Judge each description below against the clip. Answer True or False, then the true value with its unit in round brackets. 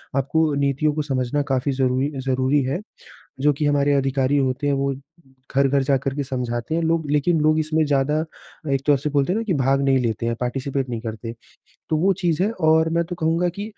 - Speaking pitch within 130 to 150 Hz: True (140 Hz)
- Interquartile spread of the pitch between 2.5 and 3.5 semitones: True (2.9 semitones)